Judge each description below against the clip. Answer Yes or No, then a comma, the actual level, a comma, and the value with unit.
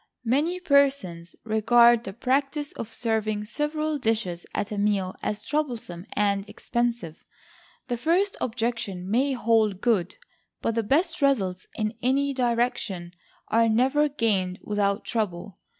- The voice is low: No, high, 230 Hz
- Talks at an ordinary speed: No, slow, 130 wpm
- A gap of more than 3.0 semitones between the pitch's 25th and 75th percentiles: Yes, average, 4.8 semitones